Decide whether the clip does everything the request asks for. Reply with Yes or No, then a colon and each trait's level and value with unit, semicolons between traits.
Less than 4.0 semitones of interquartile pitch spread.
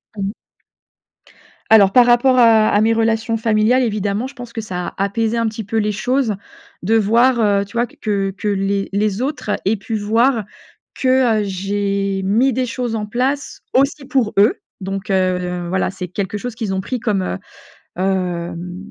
Yes: average, 3.2 semitones